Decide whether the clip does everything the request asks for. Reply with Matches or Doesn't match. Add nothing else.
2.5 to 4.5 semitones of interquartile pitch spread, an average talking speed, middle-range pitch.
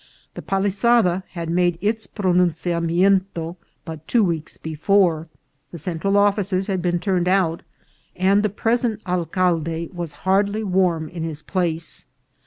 Doesn't match